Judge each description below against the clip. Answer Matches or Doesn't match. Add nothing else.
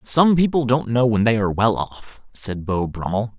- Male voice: Matches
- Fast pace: Matches